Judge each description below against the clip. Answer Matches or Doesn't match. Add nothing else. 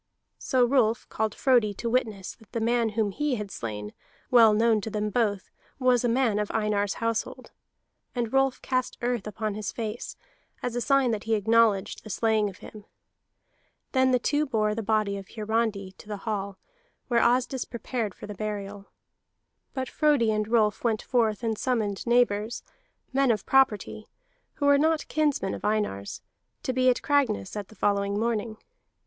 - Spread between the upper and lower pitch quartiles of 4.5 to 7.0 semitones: Doesn't match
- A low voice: Doesn't match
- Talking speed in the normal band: Matches